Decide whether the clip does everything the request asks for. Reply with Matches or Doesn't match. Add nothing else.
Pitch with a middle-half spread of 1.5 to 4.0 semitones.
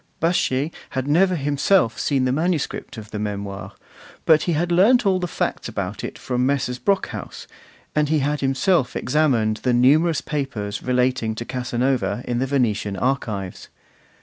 Doesn't match